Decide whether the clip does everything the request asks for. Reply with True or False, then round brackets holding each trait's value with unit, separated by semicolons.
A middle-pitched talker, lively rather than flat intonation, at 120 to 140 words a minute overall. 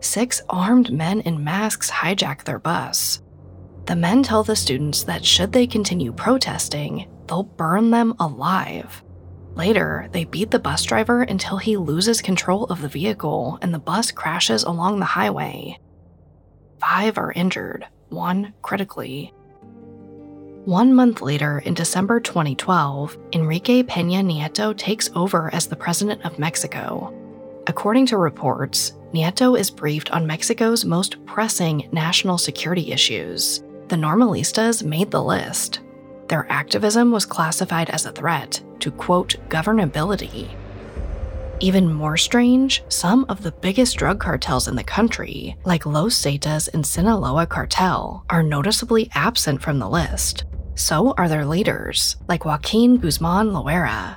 True (170 Hz; 6.4 semitones; 135 wpm)